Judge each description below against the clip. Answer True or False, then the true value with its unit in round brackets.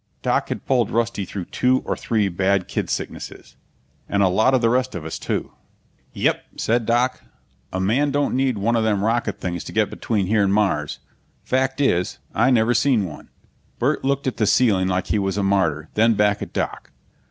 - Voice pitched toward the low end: True (110 Hz)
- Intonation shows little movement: False (4.3 semitones)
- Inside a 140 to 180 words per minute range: False (200 wpm)